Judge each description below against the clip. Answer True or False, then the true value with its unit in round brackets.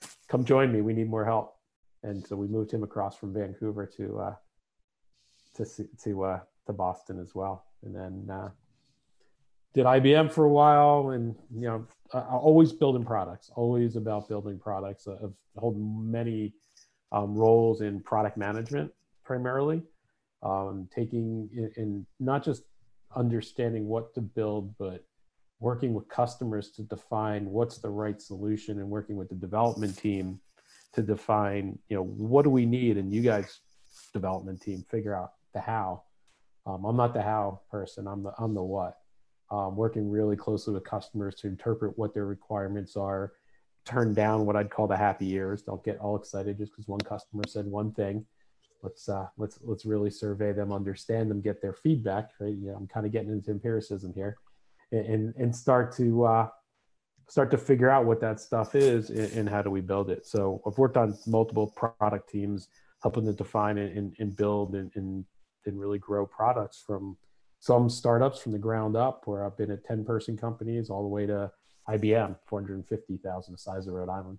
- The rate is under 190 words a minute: True (180 wpm)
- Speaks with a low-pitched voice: True (105 Hz)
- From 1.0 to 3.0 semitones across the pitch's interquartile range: True (2.4 semitones)